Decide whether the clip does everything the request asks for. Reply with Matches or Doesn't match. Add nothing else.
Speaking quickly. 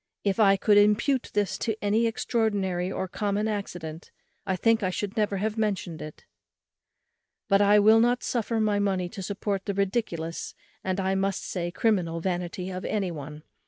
Doesn't match